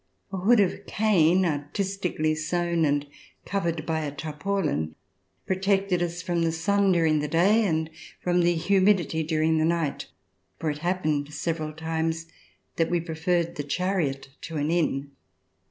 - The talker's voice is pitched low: No, medium, 165 Hz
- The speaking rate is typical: Yes, average, 150 wpm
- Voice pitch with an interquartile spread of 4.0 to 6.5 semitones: No, average, 2.7 semitones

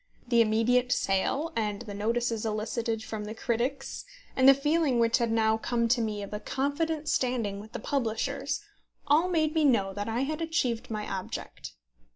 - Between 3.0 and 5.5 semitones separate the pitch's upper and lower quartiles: Yes, average, 4.2 semitones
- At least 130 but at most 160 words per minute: No, average, 180 wpm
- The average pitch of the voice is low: No, high, 235 Hz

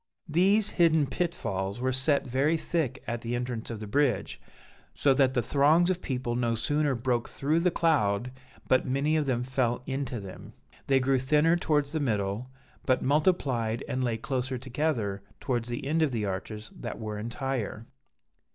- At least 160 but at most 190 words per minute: Yes, average, 170 wpm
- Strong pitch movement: No, average, 4.1 semitones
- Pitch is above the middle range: No, low, 130 Hz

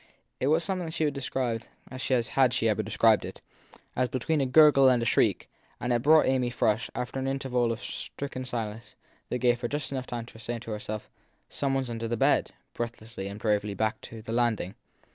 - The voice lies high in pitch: No, low, 120 Hz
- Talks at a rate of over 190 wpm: Yes, average, 200 wpm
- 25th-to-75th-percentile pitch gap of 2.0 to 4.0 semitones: Yes, average, 2.8 semitones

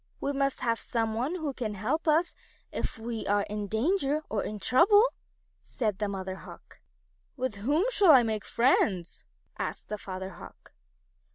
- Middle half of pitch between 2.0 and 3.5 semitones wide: No, wide, 5.6 semitones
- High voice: Yes, high, 230 Hz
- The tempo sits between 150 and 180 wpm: Yes, average, 170 wpm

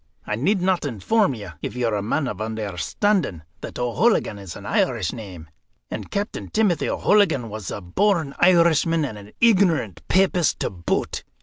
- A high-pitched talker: No, low, 135 Hz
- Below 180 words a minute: Yes, average, 165 wpm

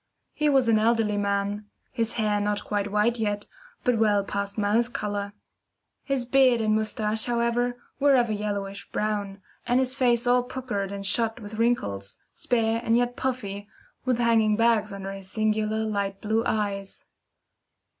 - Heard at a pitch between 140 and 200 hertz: No, high, 215 Hz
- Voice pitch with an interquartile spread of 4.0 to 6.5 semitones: No, average, 2.7 semitones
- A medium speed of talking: Yes, average, 160 wpm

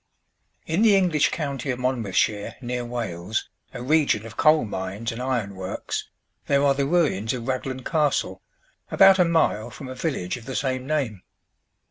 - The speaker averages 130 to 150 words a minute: No, average, 165 wpm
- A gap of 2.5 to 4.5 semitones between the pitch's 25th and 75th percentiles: No, average, 5.1 semitones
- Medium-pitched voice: No, low, 130 Hz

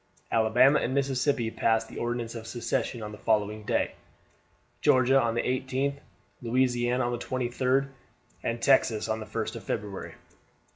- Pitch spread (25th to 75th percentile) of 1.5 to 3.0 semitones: Yes, narrow, 2.5 semitones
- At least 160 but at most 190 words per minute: No, average, 150 wpm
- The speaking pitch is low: Yes, low, 120 Hz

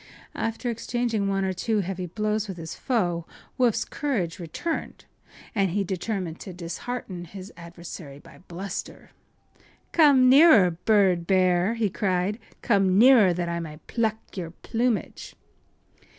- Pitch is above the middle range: Yes, high, 195 Hz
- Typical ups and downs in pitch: Yes, average, 4.5 semitones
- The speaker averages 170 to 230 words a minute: No, slow, 135 wpm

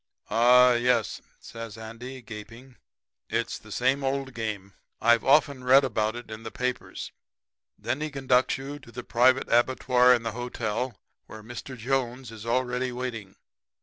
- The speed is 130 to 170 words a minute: Yes, average, 150 wpm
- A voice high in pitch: No, low, 125 Hz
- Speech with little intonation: Yes, narrow, 2.2 semitones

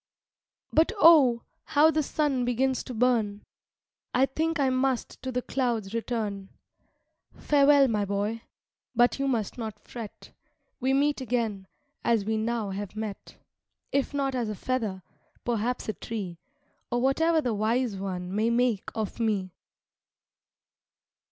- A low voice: No, high, 235 Hz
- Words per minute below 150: Yes, average, 140 wpm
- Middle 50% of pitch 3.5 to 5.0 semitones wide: Yes, average, 3.9 semitones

